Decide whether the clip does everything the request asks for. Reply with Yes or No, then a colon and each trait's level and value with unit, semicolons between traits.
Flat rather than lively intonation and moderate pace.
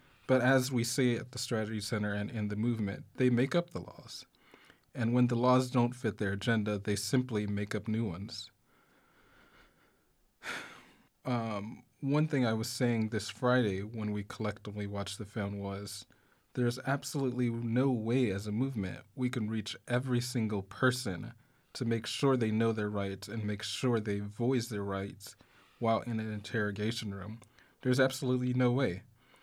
No: average, 3.3 semitones; average, 165 wpm